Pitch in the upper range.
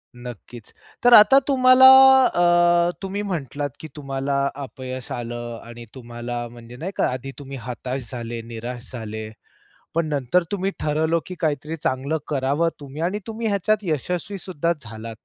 No: medium, 140 Hz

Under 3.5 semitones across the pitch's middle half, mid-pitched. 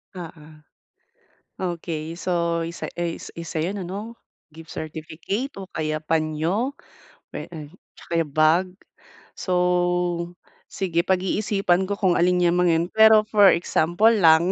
Yes: average, 2.8 semitones; medium, 175 Hz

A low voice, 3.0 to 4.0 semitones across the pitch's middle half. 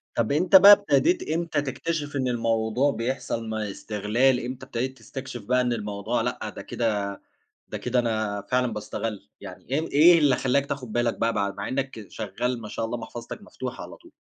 Yes: low, 120 Hz; average, 3.6 semitones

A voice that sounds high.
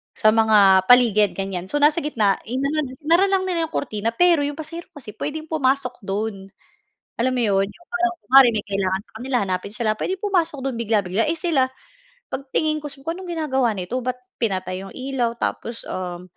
Yes: very high, 250 Hz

